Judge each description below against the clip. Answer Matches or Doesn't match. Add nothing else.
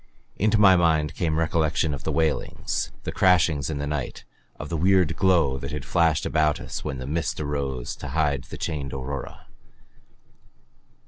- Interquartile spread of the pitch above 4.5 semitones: Doesn't match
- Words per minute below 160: Doesn't match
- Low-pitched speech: Matches